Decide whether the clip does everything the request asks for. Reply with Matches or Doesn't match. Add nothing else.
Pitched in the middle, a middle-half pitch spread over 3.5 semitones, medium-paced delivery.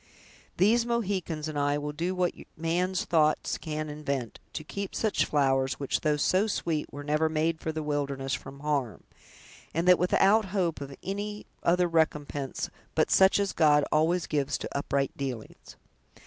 Matches